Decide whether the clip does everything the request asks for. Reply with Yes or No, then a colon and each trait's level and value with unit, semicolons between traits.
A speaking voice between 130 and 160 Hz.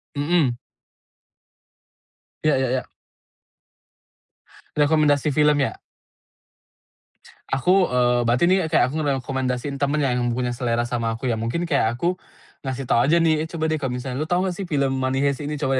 Yes: medium, 140 Hz